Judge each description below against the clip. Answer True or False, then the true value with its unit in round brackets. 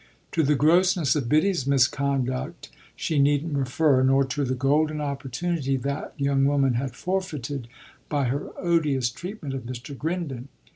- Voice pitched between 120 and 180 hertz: True (140 Hz)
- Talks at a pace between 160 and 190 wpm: False (145 wpm)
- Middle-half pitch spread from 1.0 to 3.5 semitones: True (2.7 semitones)